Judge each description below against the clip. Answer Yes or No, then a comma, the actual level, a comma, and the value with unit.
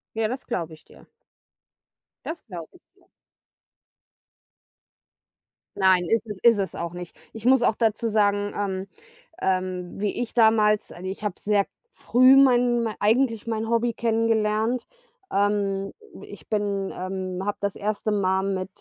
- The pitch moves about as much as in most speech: Yes, average, 3.0 semitones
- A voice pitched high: Yes, high, 210 Hz